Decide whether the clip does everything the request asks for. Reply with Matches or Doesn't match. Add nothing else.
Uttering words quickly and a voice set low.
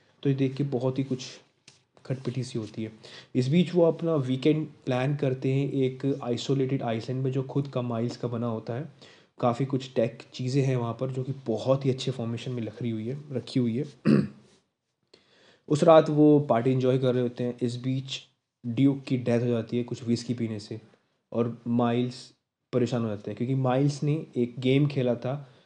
Matches